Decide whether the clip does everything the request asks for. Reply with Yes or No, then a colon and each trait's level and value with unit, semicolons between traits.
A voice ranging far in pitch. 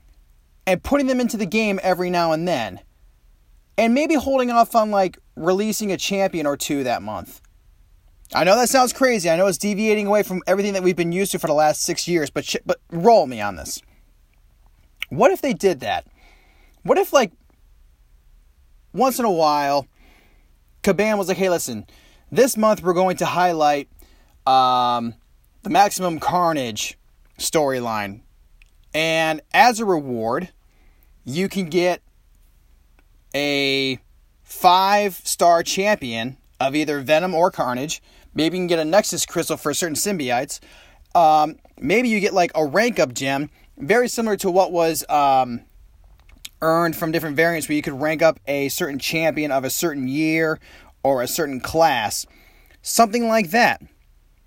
Yes: wide, 8.4 semitones